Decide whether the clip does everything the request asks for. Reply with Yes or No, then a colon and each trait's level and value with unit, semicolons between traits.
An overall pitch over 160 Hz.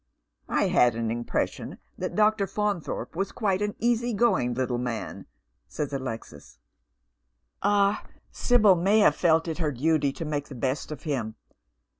No: medium, 155 Hz